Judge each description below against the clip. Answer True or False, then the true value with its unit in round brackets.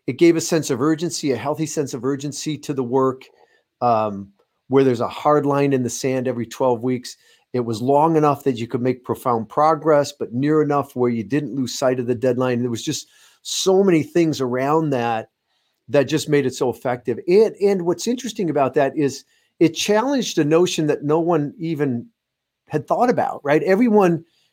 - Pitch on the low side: False (145 Hz)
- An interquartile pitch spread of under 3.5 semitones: False (4.0 semitones)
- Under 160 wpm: False (200 wpm)